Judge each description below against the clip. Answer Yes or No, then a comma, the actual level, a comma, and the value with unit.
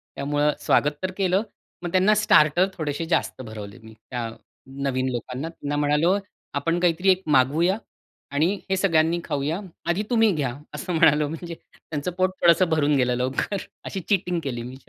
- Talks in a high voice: No, medium, 155 Hz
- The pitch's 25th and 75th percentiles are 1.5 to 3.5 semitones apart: No, average, 4.3 semitones